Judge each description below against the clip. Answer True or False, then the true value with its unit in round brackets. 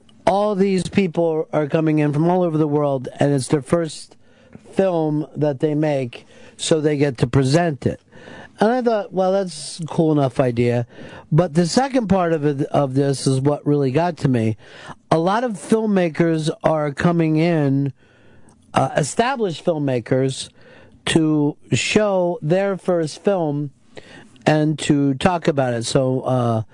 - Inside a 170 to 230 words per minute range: False (155 wpm)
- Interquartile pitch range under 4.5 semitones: True (4.0 semitones)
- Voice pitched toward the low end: False (155 Hz)